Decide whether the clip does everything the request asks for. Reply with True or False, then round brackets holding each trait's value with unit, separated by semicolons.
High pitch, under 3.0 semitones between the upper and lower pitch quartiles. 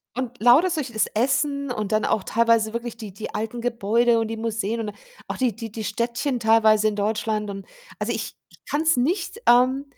True (230 Hz; 2.5 semitones)